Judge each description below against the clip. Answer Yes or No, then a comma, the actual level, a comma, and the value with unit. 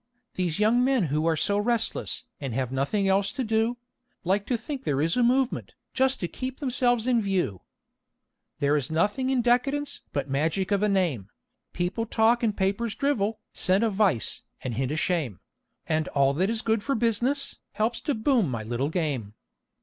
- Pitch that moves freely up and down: Yes, wide, 7.5 semitones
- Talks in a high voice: Yes, high, 205 Hz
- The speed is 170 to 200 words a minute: Yes, average, 190 wpm